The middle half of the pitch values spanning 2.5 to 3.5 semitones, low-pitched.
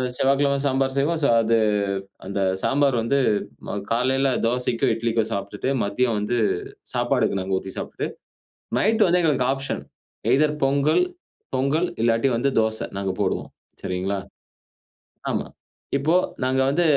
No: average, 3.9 semitones; low, 130 Hz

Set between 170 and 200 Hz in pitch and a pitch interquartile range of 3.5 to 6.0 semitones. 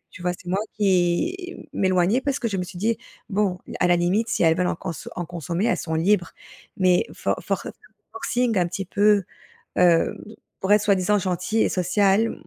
No: high, 190 Hz; average, 3.0 semitones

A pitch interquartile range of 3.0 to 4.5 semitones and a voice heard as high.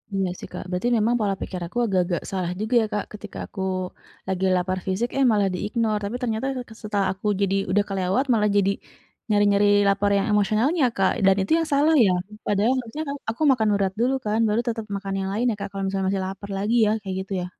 No: narrow, 2.6 semitones; high, 205 Hz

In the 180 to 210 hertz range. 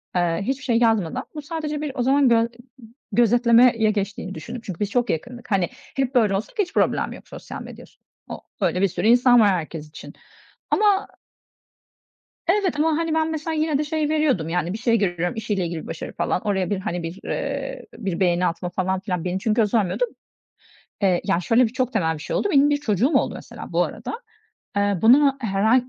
No: high, 225 Hz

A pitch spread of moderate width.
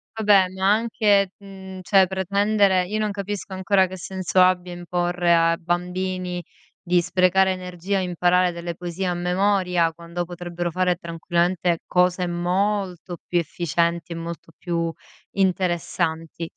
No: narrow, 1.7 semitones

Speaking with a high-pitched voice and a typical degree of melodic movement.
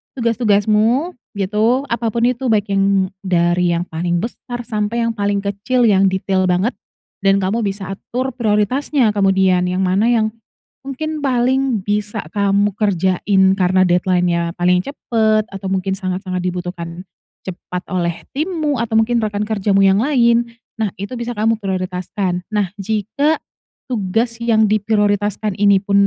Yes: high, 205 Hz; average, 3.7 semitones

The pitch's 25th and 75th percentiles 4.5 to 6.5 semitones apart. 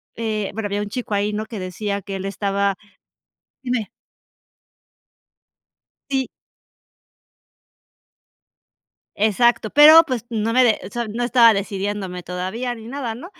No: average, 3.2 semitones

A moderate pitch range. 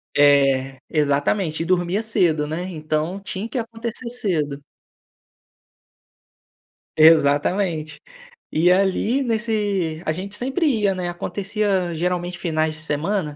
Yes: average, 4.8 semitones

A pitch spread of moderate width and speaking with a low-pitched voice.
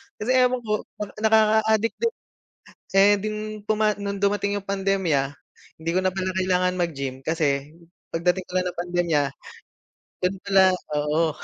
No: average, 4.0 semitones; high, 190 Hz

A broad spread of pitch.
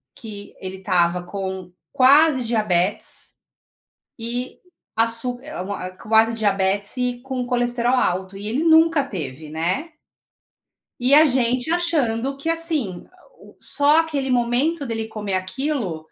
Yes: wide, 6.2 semitones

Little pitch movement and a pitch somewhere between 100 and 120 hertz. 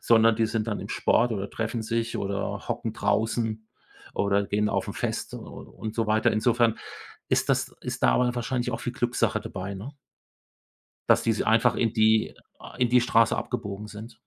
Yes: narrow, 1.7 semitones; low, 110 Hz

